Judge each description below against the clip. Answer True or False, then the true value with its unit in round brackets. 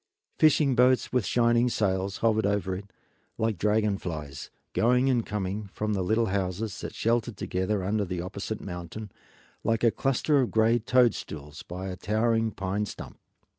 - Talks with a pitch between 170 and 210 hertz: False (105 Hz)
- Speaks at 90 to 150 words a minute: False (160 wpm)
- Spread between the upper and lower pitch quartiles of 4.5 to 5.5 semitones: False (3.6 semitones)